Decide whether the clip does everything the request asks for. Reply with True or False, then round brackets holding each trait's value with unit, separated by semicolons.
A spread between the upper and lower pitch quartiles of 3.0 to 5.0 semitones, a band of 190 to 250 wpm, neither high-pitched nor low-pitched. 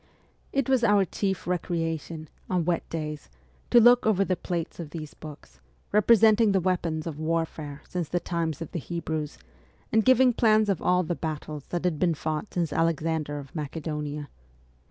False (3.7 semitones; 175 wpm; 165 Hz)